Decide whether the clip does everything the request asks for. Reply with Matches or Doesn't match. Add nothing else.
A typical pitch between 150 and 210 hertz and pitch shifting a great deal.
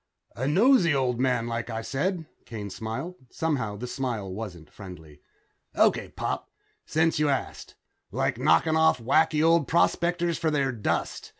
Doesn't match